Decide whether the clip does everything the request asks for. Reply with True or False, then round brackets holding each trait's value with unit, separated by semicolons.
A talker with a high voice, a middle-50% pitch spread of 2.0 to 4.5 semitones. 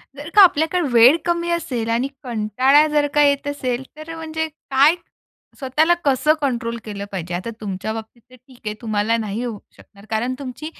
False (255 Hz; 5.2 semitones)